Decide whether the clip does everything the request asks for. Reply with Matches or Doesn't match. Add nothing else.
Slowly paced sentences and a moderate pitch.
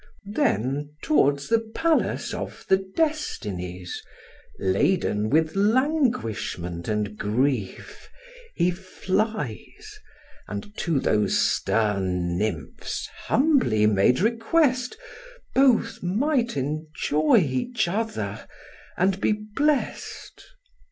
Matches